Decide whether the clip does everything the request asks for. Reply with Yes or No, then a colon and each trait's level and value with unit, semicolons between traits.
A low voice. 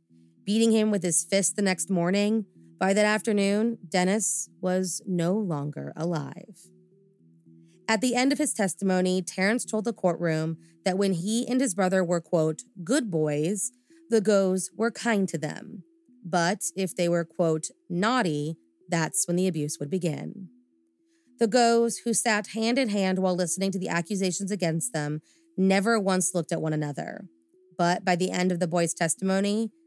No: high, 190 Hz